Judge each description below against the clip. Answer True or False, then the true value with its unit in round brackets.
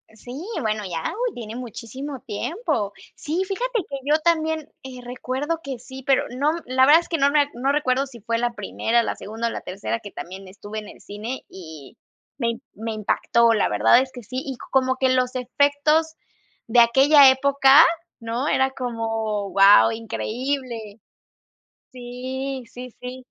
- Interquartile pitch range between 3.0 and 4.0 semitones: True (3.6 semitones)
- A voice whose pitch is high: True (250 Hz)